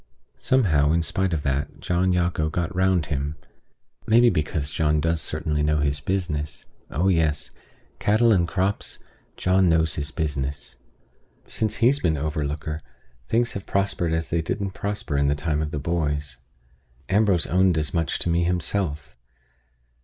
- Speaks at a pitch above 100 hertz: No, very low, 80 Hz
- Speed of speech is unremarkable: Yes, average, 155 wpm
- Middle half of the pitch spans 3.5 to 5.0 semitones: Yes, average, 4.0 semitones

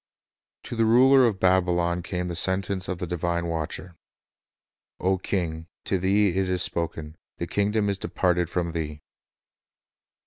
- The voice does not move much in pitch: Yes, narrow, 2.2 semitones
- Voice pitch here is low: Yes, very low, 90 Hz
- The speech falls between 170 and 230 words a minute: No, average, 160 wpm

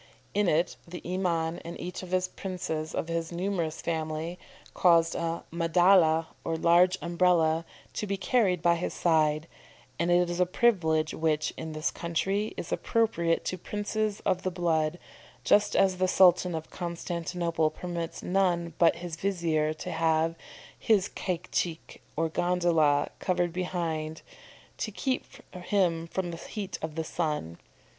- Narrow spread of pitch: Yes, narrow, 2.1 semitones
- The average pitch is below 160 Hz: No, medium, 170 Hz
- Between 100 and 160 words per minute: Yes, average, 150 wpm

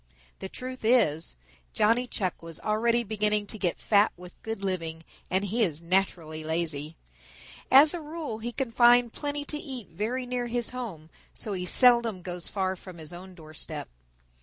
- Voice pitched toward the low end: No, high, 210 Hz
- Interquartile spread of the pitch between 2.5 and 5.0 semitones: No, wide, 5.6 semitones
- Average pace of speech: Yes, average, 170 wpm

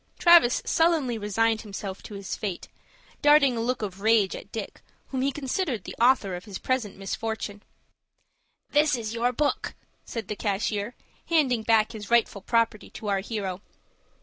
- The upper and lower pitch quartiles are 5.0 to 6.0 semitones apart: No, average, 3.8 semitones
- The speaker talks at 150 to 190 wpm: Yes, average, 160 wpm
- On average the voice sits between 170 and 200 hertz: No, high, 225 Hz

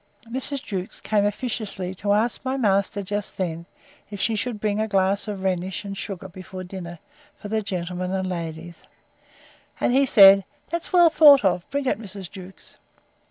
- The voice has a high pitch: Yes, high, 200 Hz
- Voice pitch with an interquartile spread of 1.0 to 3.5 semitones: Yes, average, 2.9 semitones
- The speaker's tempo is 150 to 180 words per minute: Yes, average, 170 wpm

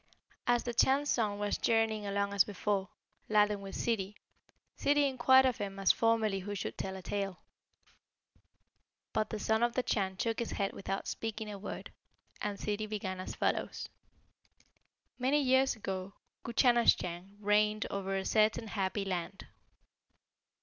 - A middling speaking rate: Yes, average, 150 wpm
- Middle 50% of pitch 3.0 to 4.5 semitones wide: No, narrow, 2.6 semitones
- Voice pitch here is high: Yes, high, 210 Hz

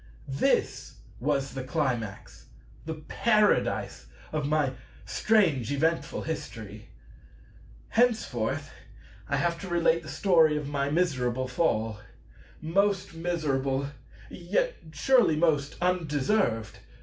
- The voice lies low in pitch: No, medium, 155 Hz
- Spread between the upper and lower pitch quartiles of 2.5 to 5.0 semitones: Yes, average, 4.5 semitones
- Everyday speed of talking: No, slow, 95 wpm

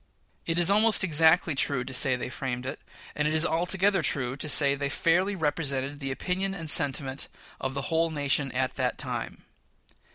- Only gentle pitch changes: No, average, 3.8 semitones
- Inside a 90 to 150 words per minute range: No, average, 185 wpm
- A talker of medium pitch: Yes, medium, 150 Hz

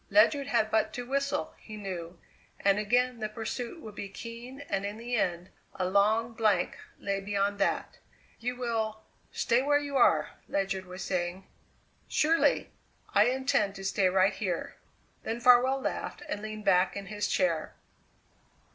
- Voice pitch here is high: Yes, high, 215 Hz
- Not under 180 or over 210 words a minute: No, average, 155 wpm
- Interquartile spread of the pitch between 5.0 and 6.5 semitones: No, average, 3.8 semitones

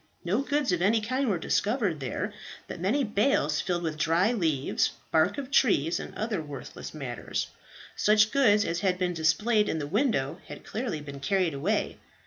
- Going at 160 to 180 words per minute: Yes, average, 175 wpm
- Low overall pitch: No, medium, 185 Hz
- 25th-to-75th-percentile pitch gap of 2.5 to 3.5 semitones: No, wide, 5.6 semitones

